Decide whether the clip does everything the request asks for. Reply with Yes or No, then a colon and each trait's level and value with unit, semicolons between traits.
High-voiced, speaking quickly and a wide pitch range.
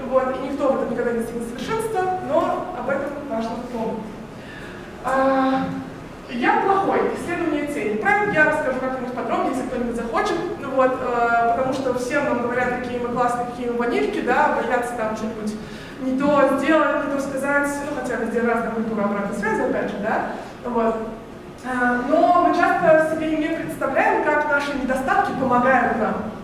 No: very high, 260 Hz; fast, 165 wpm; average, 4.0 semitones